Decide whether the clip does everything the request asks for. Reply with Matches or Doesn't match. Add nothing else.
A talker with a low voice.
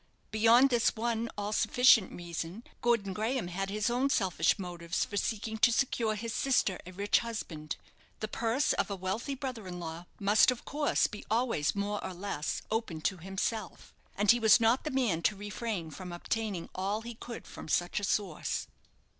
Doesn't match